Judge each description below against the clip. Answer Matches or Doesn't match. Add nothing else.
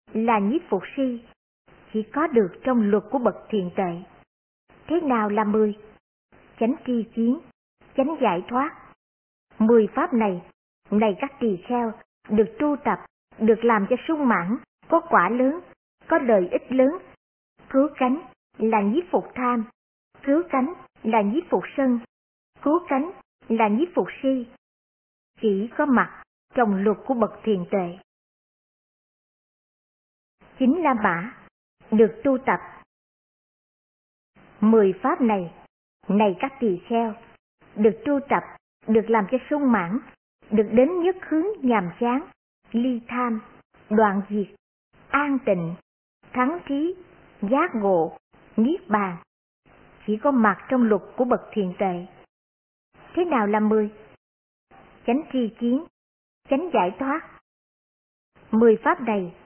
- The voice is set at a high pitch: Matches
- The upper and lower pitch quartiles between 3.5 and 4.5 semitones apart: Matches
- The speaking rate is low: Matches